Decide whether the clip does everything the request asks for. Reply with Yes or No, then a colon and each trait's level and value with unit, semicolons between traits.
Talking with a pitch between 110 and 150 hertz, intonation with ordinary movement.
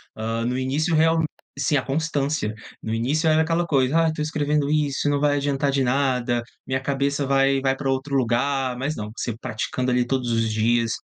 Yes: low, 135 Hz; average, 3.0 semitones